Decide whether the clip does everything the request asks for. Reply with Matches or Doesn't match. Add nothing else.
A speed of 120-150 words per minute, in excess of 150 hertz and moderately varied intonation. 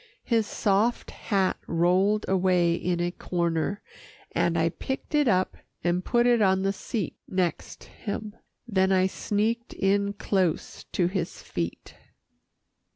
Matches